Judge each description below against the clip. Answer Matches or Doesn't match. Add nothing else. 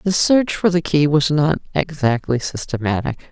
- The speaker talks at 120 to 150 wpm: Doesn't match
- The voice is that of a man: Doesn't match